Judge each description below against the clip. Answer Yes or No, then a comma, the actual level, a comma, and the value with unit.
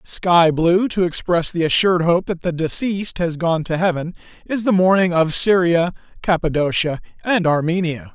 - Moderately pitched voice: Yes, medium, 175 Hz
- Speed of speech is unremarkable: Yes, average, 160 wpm